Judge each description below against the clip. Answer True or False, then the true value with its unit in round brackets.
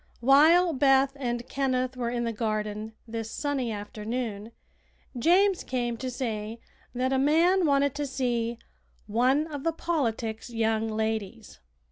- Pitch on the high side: True (245 Hz)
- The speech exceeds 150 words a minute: False (135 wpm)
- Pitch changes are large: False (3.8 semitones)